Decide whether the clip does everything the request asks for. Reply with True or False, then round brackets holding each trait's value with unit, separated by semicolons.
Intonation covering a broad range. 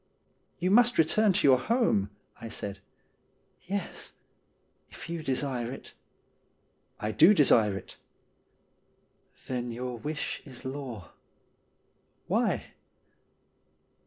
True (6.4 semitones)